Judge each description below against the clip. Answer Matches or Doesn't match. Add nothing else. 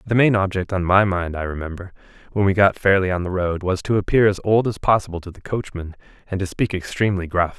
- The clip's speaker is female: Doesn't match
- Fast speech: Matches